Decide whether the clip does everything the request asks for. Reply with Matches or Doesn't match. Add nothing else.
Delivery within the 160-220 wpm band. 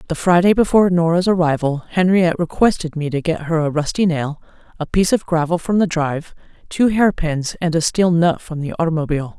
Matches